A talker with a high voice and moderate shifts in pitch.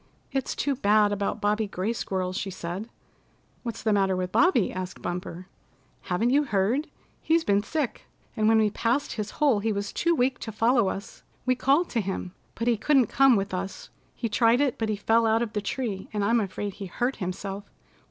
Yes: high, 215 Hz; average, 3.8 semitones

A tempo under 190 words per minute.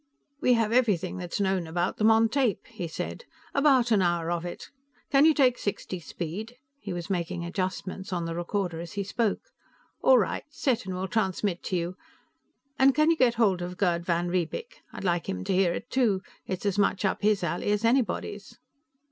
No: average, 200 wpm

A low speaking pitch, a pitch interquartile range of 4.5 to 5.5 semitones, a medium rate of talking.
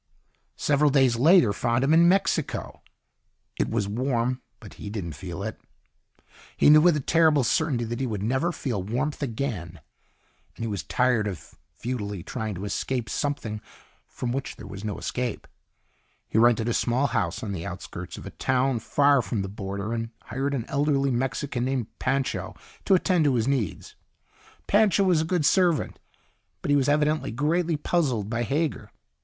Yes: low, 125 Hz; average, 5.0 semitones; average, 170 wpm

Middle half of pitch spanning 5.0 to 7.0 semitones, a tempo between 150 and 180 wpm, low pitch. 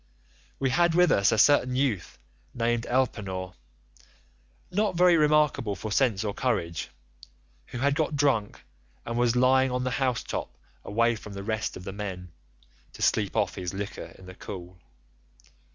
Yes: average, 5.3 semitones; average, 160 wpm; low, 120 Hz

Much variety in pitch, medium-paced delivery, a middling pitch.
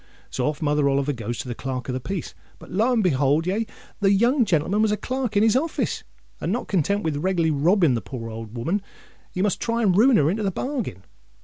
No: wide, 7.3 semitones; fast, 230 wpm; medium, 180 Hz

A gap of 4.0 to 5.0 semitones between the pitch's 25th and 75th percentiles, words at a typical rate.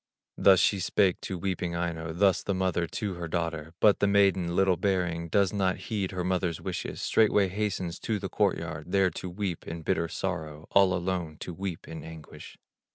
No: narrow, 2.6 semitones; average, 190 wpm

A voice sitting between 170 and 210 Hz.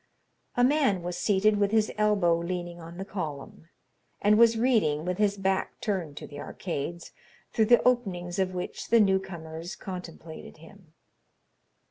Yes: high, 190 Hz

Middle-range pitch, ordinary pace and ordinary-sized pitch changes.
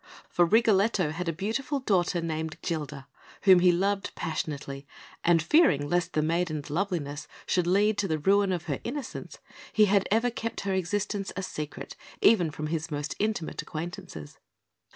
Yes: medium, 175 Hz; average, 160 wpm; average, 4.6 semitones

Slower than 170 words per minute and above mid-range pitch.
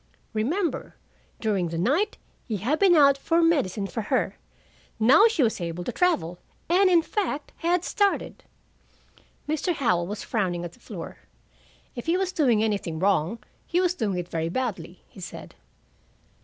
Yes: average, 160 wpm; high, 240 Hz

